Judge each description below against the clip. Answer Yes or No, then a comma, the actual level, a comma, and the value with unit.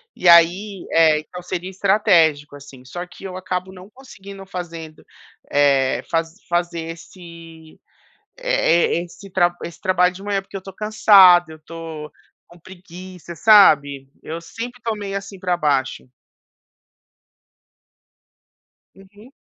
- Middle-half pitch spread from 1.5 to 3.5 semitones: Yes, average, 3.0 semitones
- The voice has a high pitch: No, medium, 180 Hz